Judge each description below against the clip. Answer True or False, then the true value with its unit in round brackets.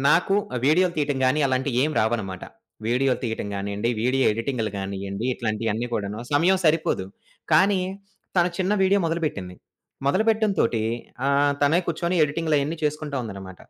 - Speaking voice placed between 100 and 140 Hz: True (135 Hz)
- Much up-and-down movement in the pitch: True (6.8 semitones)